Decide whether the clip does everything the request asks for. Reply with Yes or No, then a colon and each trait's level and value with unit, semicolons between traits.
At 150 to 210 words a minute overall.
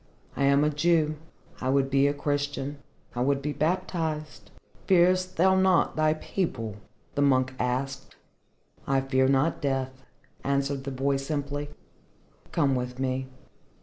No: average, 140 wpm